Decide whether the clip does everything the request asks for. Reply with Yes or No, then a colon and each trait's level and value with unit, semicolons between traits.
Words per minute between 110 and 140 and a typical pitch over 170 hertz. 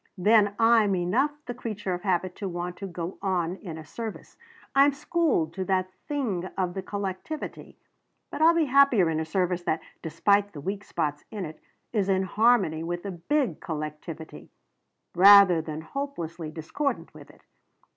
No: average, 165 wpm; high, 190 Hz